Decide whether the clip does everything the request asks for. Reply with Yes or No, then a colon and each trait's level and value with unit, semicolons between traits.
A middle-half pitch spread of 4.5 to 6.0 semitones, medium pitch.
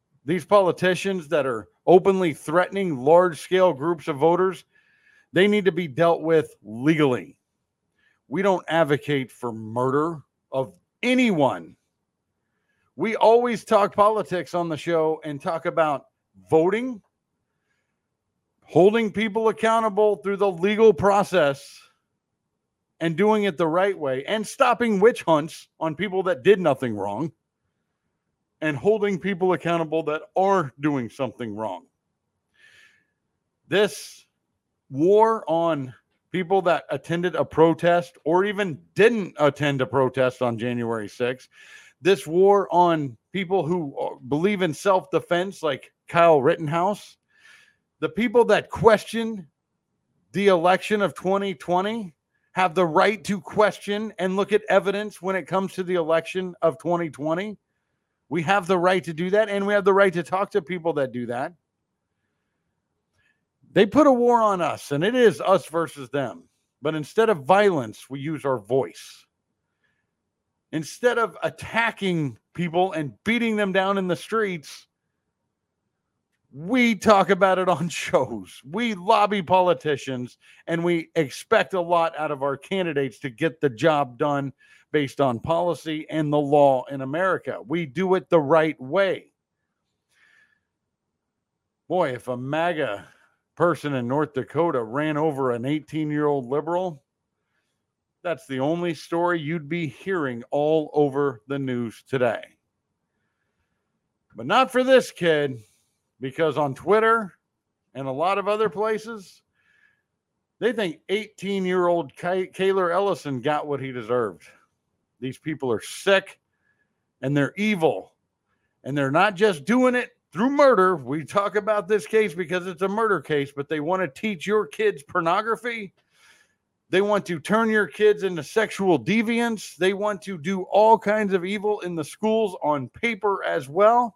Yes: wide, 5.4 semitones; medium, 175 Hz